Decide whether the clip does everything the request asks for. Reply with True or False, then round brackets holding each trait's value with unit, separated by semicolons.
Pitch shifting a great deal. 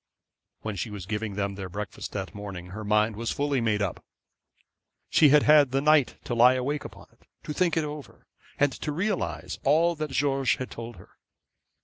True (6.1 semitones)